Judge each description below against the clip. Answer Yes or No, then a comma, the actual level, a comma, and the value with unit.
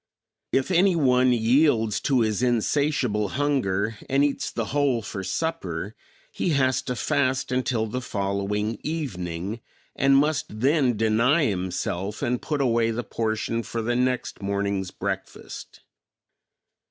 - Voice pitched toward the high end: No, low, 120 Hz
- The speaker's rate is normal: No, slow, 130 wpm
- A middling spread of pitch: Yes, average, 4.7 semitones